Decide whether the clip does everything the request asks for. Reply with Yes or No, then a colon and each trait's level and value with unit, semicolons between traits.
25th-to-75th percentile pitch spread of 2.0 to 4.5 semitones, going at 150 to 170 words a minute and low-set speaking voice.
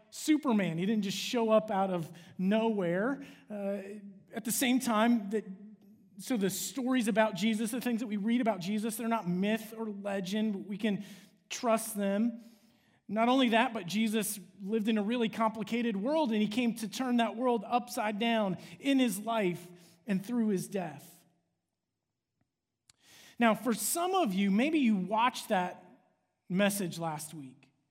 No: average, 3.0 semitones; average, 165 wpm; high, 215 Hz